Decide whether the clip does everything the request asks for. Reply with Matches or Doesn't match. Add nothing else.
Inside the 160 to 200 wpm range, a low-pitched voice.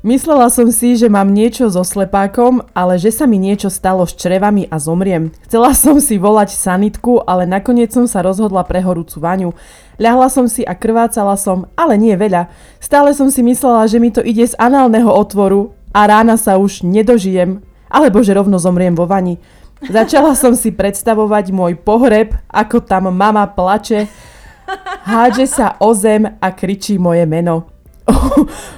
Doesn't match